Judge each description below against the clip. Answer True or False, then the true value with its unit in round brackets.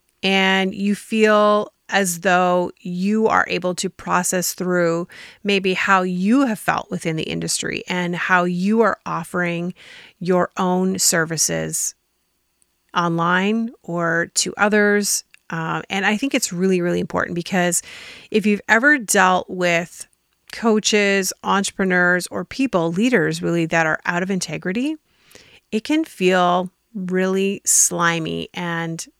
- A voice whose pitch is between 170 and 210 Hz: True (185 Hz)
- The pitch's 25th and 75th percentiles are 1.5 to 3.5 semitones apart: True (2.7 semitones)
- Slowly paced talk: True (125 wpm)